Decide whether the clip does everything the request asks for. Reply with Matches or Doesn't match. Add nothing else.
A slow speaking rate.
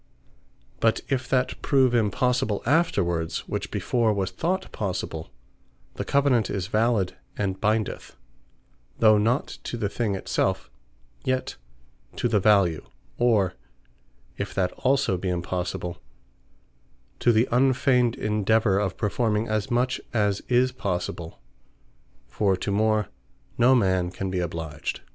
Matches